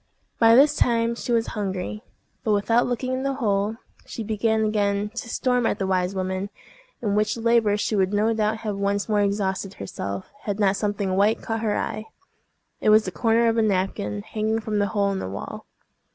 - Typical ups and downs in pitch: No, narrow, 2.2 semitones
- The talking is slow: No, average, 200 wpm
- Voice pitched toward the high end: Yes, high, 210 Hz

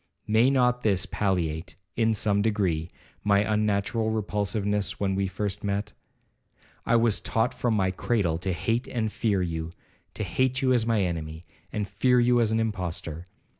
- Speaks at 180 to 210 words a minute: No, average, 160 wpm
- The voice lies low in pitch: Yes, low, 105 Hz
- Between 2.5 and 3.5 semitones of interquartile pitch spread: Yes, average, 3.1 semitones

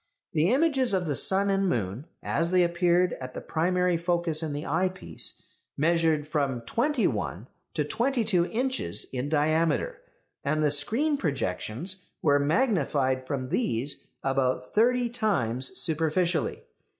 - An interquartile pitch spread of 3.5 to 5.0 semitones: No, wide, 5.4 semitones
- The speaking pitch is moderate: Yes, medium, 165 Hz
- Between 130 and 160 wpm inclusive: Yes, average, 140 wpm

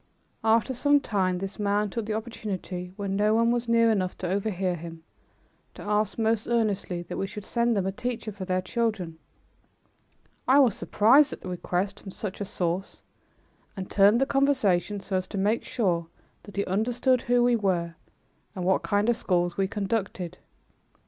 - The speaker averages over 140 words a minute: Yes, average, 180 wpm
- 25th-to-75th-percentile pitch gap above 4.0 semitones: No, average, 3.6 semitones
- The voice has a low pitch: No, high, 205 Hz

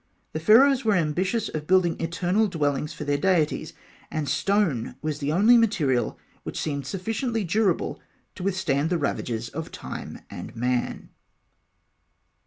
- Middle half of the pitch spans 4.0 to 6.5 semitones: Yes, wide, 5.5 semitones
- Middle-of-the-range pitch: Yes, medium, 170 Hz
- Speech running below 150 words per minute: Yes, average, 140 wpm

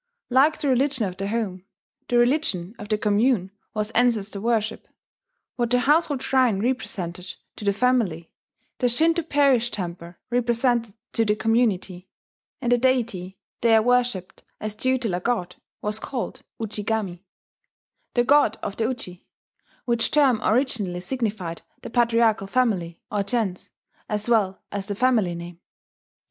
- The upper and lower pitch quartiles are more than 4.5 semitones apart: No, average, 4.1 semitones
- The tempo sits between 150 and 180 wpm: No, average, 140 wpm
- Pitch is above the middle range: Yes, high, 225 Hz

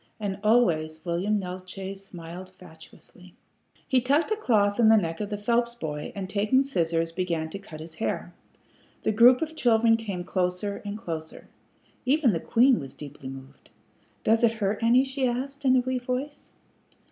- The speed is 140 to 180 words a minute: Yes, average, 170 wpm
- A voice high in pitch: Yes, high, 205 Hz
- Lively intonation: Yes, wide, 5.9 semitones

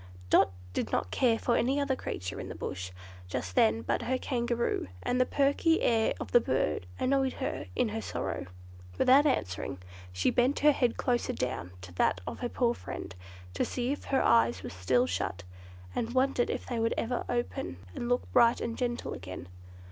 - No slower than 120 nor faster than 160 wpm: No, average, 190 wpm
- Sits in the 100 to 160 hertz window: No, high, 235 Hz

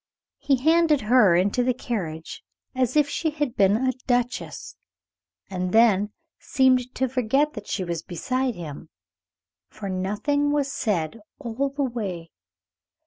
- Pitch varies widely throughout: Yes, wide, 5.7 semitones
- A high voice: Yes, high, 245 Hz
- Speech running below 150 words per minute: Yes, average, 140 wpm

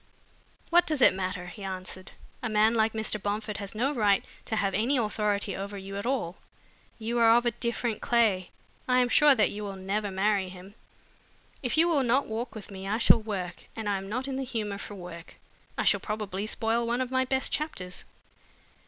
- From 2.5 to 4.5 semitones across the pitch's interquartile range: Yes, average, 3.4 semitones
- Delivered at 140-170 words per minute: No, fast, 205 wpm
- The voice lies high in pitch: Yes, high, 215 Hz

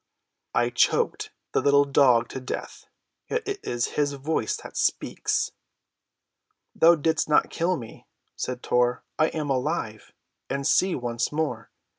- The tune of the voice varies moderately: Yes, average, 4.5 semitones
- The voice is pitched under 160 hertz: Yes, medium, 140 Hz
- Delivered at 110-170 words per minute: Yes, average, 140 wpm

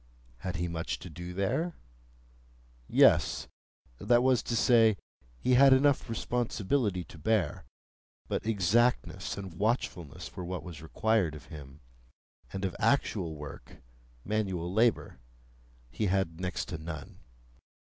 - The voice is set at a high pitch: No, very low, 90 Hz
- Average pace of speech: No, slow, 120 wpm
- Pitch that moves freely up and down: Yes, wide, 6.2 semitones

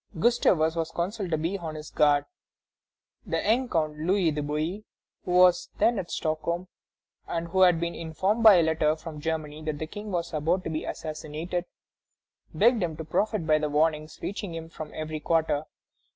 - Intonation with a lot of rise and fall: No, average, 2.8 semitones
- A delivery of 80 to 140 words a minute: No, average, 180 wpm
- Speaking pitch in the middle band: Yes, medium, 165 Hz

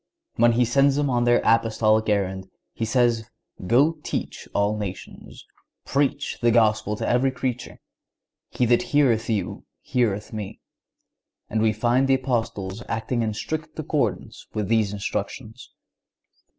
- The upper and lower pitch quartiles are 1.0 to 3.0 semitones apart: Yes, average, 2.7 semitones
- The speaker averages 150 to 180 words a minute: No, slow, 135 wpm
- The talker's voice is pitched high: No, low, 115 Hz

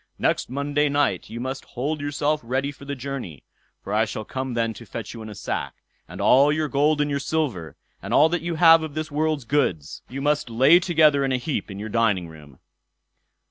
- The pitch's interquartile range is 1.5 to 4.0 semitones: No, average, 4.6 semitones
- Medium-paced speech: No, fast, 220 wpm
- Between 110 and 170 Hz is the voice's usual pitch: Yes, medium, 140 Hz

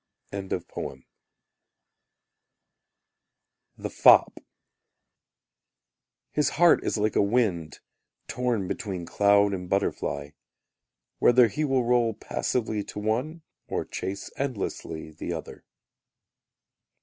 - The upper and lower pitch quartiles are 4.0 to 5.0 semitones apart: Yes, average, 4.6 semitones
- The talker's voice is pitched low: Yes, low, 105 Hz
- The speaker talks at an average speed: No, slow, 90 wpm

